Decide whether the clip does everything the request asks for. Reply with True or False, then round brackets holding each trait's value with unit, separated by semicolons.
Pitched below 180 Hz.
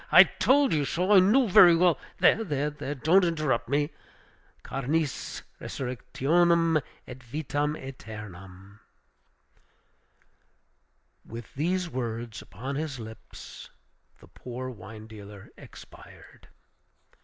True (135 Hz)